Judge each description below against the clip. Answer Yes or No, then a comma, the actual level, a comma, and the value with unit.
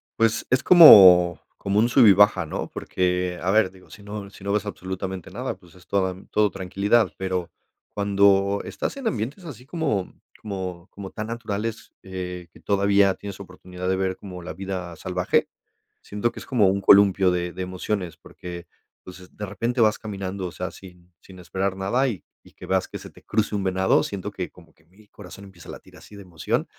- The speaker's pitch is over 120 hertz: No, very low, 95 Hz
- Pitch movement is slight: Yes, narrow, 2.2 semitones